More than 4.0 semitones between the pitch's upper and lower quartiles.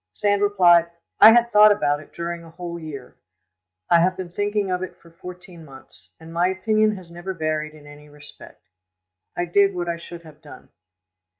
No: average, 3.2 semitones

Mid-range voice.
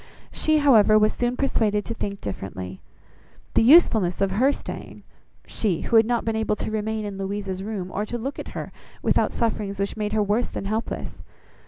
No: high, 215 Hz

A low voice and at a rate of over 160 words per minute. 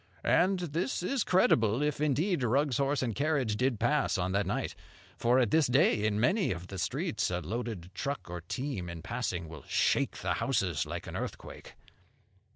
Yes: low, 125 Hz; average, 180 wpm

